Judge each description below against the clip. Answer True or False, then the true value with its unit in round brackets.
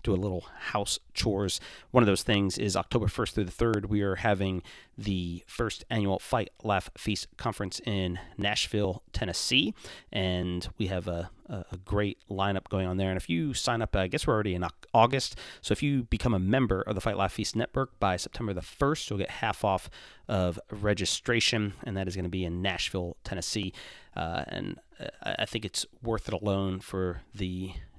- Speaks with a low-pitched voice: True (100 Hz)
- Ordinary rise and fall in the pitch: True (3.0 semitones)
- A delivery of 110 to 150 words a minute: False (195 wpm)